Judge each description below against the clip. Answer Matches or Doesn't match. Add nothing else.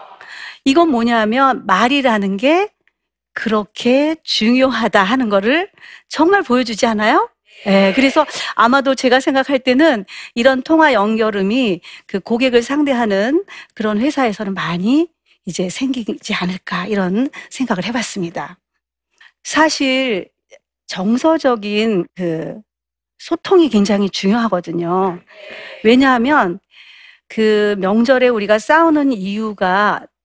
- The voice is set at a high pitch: Matches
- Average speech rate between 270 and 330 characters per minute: Doesn't match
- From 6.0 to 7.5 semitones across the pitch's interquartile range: Doesn't match